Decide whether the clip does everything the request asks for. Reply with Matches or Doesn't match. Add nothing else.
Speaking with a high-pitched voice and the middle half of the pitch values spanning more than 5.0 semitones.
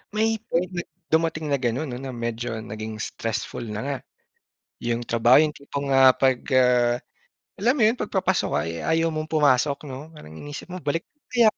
Doesn't match